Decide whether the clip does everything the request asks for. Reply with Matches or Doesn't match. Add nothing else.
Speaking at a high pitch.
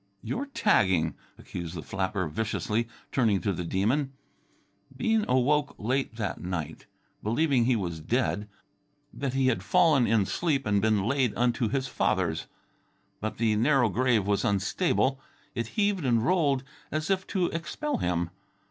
Doesn't match